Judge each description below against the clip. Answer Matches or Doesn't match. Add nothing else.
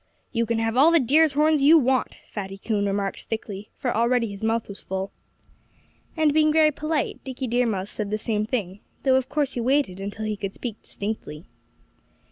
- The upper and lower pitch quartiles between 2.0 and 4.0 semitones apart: Doesn't match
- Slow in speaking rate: Doesn't match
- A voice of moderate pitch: Doesn't match